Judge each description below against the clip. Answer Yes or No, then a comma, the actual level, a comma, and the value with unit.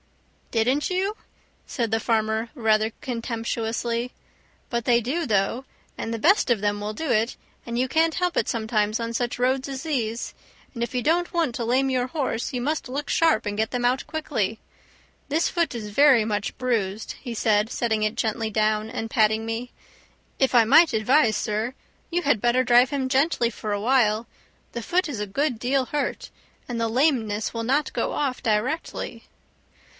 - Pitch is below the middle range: No, high, 240 Hz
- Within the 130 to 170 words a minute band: No, average, 180 wpm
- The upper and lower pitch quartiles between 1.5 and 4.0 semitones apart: Yes, average, 3.6 semitones